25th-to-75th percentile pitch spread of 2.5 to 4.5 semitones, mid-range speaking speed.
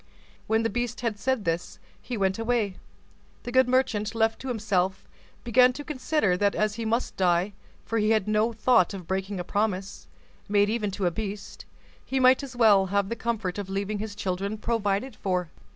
Yes: average, 3.1 semitones; average, 185 wpm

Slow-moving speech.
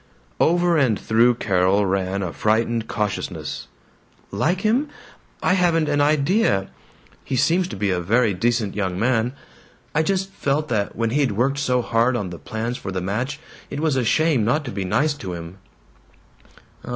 No: average, 175 wpm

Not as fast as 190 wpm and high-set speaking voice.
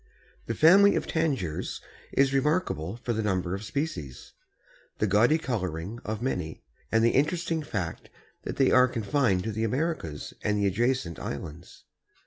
No: average, 155 wpm; low, 115 Hz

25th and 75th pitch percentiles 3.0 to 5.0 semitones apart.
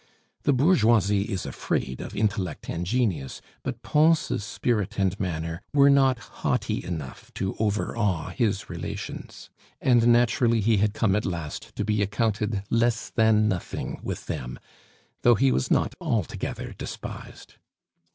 Yes: average, 3.9 semitones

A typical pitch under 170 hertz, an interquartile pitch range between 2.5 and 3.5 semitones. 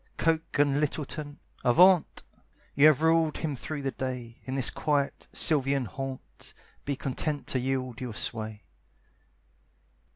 Yes: medium, 140 Hz; average, 3.0 semitones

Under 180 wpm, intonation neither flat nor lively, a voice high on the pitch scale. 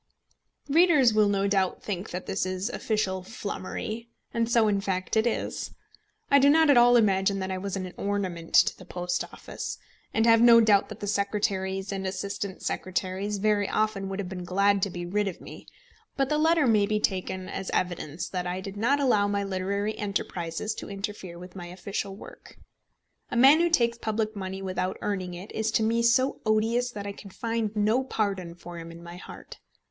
No: average, 200 wpm; average, 3.0 semitones; high, 200 Hz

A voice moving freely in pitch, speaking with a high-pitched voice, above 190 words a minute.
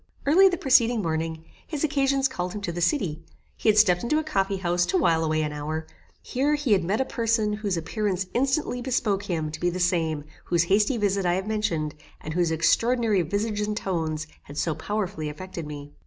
Yes: wide, 5.8 semitones; high, 195 Hz; fast, 205 wpm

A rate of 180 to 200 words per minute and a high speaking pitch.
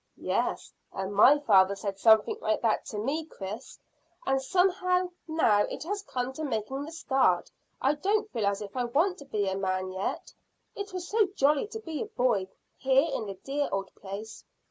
Yes: average, 190 wpm; very high, 260 Hz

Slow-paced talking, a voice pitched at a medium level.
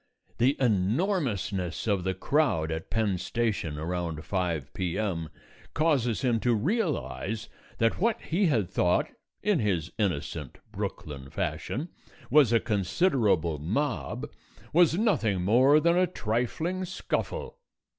No: slow, 120 wpm; low, 110 Hz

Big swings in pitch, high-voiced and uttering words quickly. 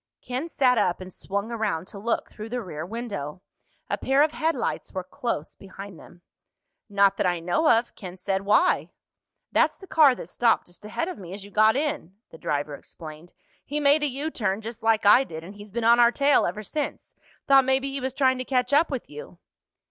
Yes: wide, 6.0 semitones; high, 220 Hz; fast, 215 wpm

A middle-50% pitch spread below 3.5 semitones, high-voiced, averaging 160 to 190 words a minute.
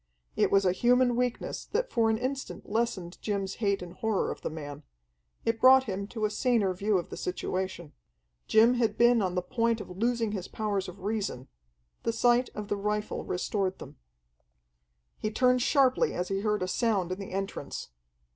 No: average, 3.8 semitones; high, 210 Hz; average, 185 wpm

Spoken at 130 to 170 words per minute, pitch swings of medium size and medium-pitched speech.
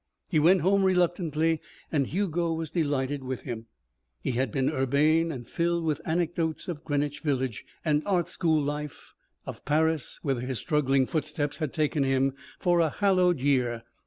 Yes: average, 160 wpm; average, 3.6 semitones; medium, 150 Hz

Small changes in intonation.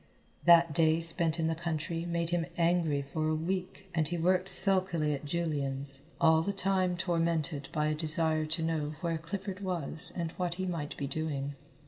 Yes: narrow, 2.1 semitones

